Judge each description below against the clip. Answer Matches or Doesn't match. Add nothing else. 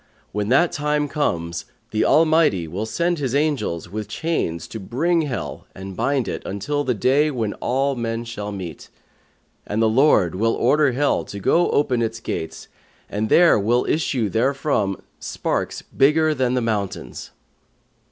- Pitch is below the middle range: Matches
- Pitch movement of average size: Doesn't match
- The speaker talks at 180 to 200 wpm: Doesn't match